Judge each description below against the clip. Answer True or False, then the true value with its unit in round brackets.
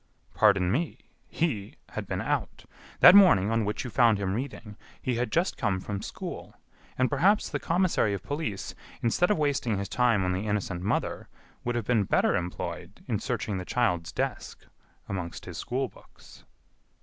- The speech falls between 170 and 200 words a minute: True (175 wpm)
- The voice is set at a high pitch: False (110 Hz)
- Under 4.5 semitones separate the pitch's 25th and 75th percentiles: False (5.3 semitones)